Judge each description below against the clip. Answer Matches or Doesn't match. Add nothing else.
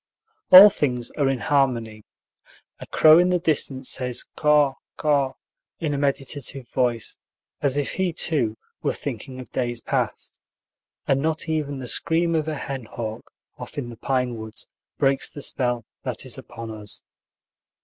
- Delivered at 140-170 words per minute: Matches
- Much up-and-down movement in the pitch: Doesn't match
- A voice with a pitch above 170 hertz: Doesn't match